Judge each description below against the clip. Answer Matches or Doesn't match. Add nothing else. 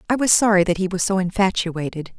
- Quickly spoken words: Matches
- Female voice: Matches